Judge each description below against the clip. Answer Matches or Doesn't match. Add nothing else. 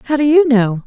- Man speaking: Doesn't match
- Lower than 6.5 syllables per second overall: Matches